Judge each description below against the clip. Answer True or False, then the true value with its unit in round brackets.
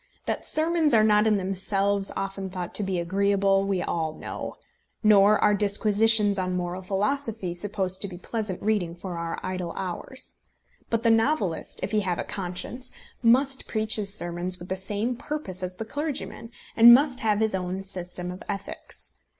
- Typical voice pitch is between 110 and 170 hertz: False (200 Hz)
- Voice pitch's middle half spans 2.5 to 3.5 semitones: True (3.2 semitones)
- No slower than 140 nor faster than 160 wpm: False (175 wpm)